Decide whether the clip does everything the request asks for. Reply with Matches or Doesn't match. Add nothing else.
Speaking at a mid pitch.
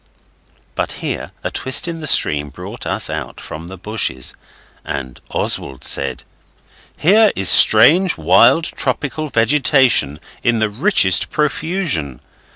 Doesn't match